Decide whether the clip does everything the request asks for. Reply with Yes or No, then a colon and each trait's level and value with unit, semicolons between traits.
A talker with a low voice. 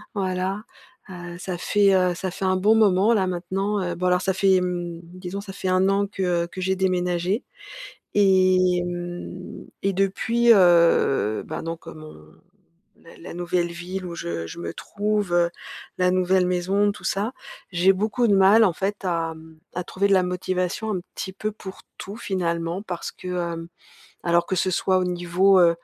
No: medium, 185 Hz